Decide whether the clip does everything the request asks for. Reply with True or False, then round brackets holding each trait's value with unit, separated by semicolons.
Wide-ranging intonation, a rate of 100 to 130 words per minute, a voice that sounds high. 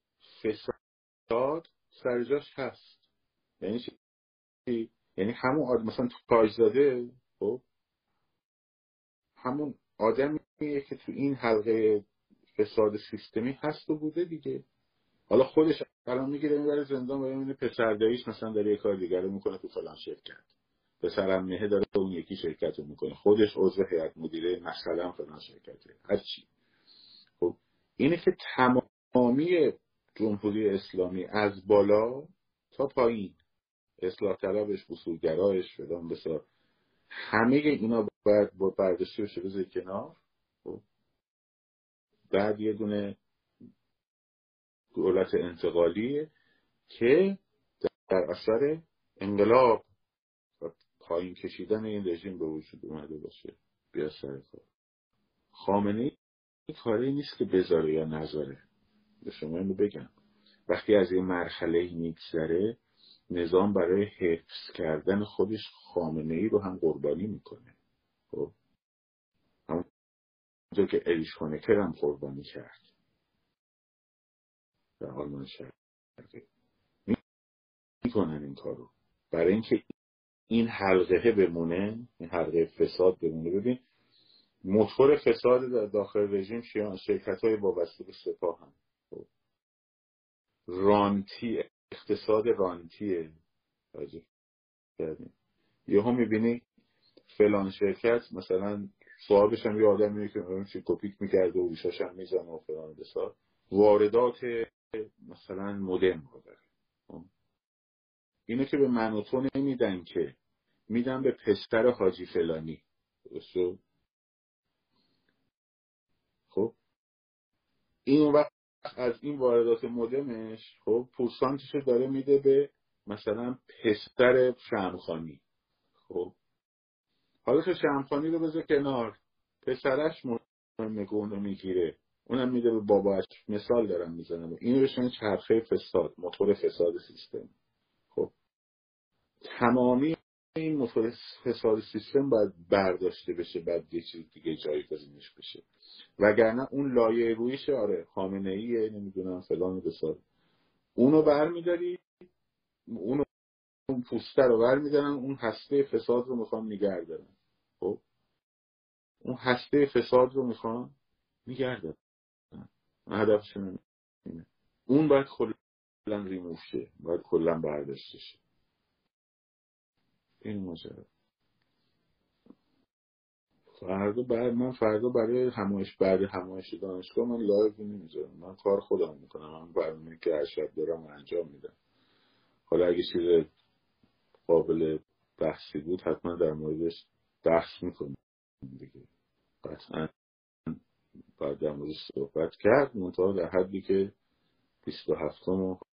False (7.2 semitones; 110 wpm; 110 Hz)